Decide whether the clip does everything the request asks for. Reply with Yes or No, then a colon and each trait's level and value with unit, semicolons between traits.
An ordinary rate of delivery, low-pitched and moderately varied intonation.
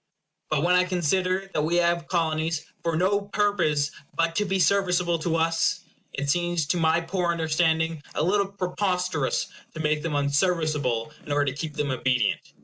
No: average, 170 wpm; medium, 165 Hz; average, 3.0 semitones